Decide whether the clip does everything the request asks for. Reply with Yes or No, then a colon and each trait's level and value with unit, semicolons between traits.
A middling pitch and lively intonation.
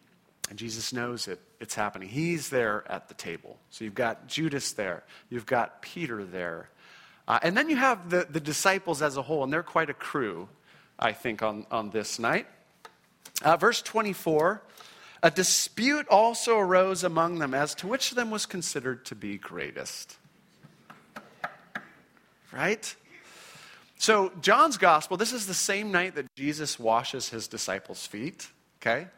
Yes: medium, 155 Hz; wide, 8.7 semitones